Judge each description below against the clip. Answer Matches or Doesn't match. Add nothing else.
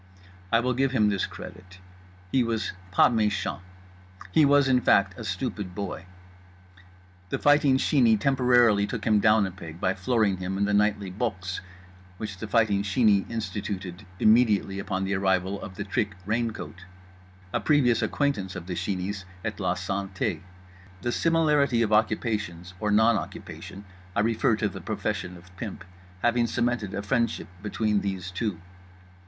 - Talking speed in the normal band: Matches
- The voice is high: Doesn't match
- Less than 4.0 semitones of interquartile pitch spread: Matches